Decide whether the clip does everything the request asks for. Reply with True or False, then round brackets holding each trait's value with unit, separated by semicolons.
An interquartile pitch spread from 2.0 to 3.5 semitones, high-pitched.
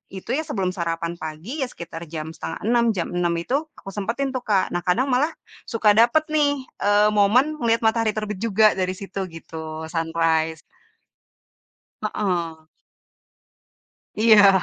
False (5.4 semitones; 200 Hz)